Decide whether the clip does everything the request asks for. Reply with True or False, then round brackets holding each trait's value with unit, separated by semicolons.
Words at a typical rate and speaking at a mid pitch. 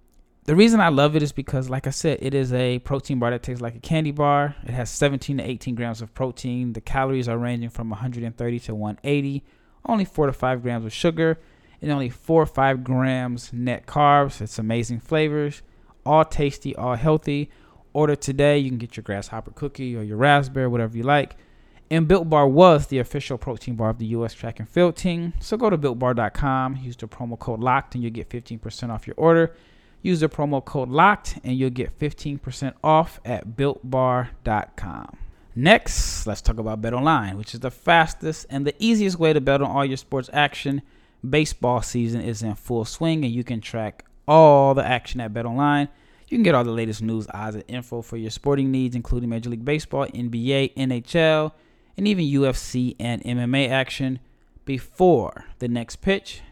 False (195 wpm; 130 Hz)